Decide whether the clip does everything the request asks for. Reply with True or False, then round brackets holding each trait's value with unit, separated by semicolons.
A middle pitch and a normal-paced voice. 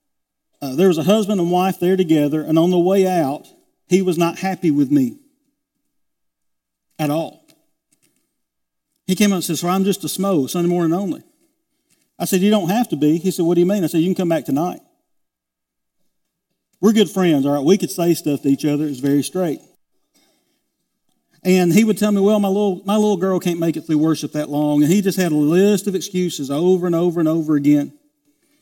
False (175 Hz; 215 wpm)